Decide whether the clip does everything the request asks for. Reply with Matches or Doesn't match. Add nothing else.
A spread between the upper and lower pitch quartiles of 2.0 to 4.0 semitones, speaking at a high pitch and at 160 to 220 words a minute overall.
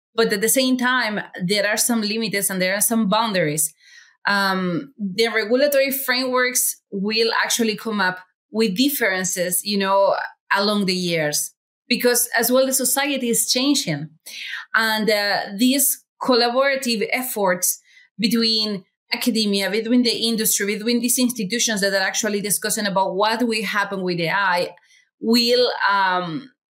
Doesn't match